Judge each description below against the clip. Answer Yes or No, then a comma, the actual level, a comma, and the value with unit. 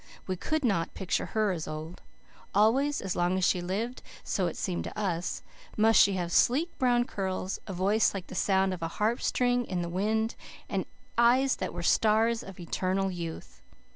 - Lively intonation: No, average, 4.0 semitones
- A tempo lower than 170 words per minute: No, average, 185 wpm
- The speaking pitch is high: Yes, high, 195 Hz